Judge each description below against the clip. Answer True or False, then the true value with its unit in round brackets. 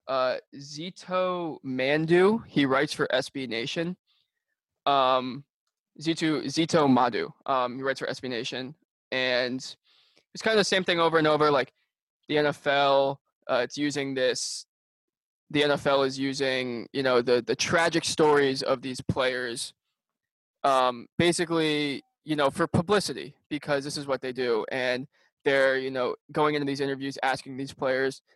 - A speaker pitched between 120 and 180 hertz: True (140 Hz)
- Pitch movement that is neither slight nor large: True (3.4 semitones)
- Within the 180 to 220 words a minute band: False (150 wpm)